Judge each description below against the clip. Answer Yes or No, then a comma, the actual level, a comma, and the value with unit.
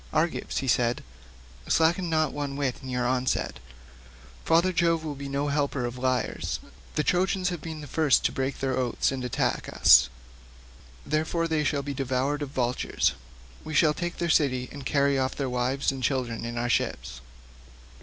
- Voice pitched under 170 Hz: Yes, medium, 140 Hz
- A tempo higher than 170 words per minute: Yes, average, 180 wpm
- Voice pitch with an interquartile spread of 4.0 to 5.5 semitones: No, average, 3.6 semitones